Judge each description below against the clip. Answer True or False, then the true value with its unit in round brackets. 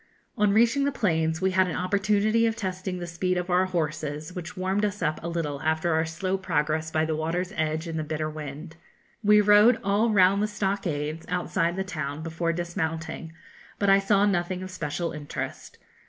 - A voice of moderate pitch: True (180 Hz)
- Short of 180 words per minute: False (190 wpm)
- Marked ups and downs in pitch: False (3.7 semitones)